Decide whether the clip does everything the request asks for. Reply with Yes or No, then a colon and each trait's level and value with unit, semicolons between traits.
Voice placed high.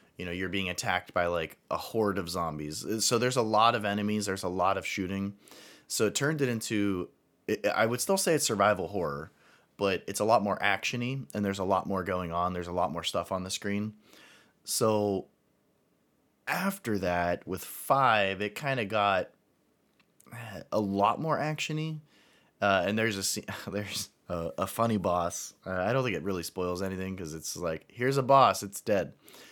No: low, 100 Hz